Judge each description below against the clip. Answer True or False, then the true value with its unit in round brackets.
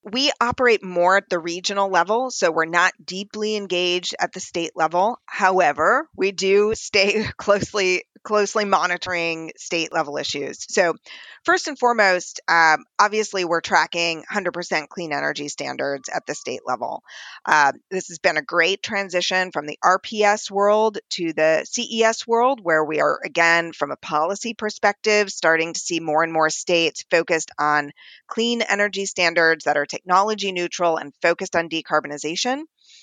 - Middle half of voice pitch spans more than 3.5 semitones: True (4.1 semitones)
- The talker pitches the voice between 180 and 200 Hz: True (185 Hz)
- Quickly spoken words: False (155 wpm)